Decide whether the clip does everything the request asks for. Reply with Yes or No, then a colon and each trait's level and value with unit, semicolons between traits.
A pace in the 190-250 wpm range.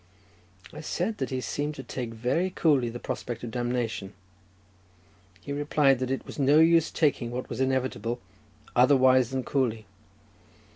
No: average, 155 wpm